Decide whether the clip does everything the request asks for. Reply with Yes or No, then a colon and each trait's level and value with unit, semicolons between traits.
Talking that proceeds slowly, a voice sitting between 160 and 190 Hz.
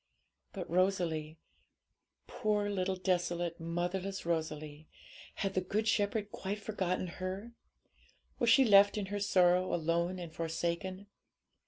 Yes: slow, 120 wpm; medium, 185 Hz